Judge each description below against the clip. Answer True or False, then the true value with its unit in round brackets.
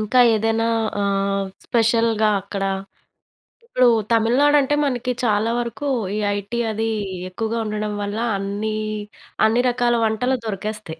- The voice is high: True (220 Hz)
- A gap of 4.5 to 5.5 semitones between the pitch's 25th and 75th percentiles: False (2.5 semitones)